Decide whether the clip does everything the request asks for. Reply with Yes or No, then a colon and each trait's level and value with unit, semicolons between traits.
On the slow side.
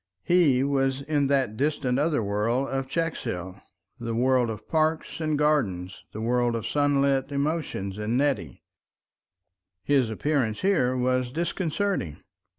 Yes: slow, 130 wpm